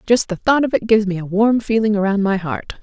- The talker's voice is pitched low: No, high, 210 Hz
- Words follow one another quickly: Yes, fast, 275 wpm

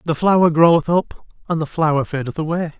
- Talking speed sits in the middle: Yes, average, 195 wpm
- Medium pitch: Yes, medium, 160 Hz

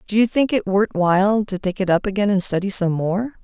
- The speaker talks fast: Yes, fast, 260 wpm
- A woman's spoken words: Yes, female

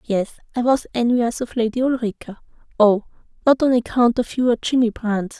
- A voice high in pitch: Yes, high, 235 Hz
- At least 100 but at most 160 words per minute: Yes, average, 155 wpm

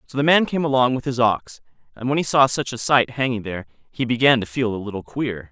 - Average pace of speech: No, fast, 260 wpm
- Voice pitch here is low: Yes, low, 120 Hz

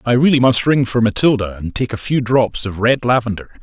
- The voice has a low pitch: Yes, low, 120 Hz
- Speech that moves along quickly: Yes, fast, 230 wpm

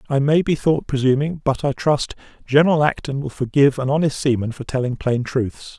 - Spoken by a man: Yes, male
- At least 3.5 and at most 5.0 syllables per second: No, 5.5 syllables/s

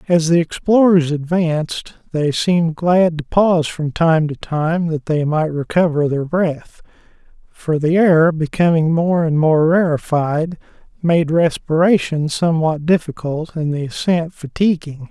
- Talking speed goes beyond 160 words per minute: No, average, 140 wpm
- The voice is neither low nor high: Yes, medium, 160 Hz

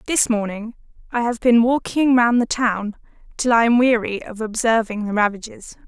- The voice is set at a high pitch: Yes, high, 230 Hz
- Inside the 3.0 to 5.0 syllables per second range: Yes, 4.9 syllables/s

